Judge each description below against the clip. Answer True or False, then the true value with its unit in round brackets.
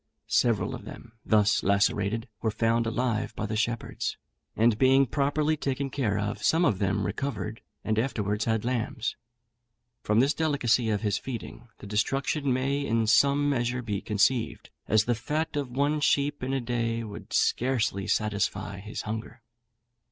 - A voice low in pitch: True (115 Hz)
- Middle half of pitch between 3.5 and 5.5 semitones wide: True (4.1 semitones)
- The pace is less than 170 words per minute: True (160 wpm)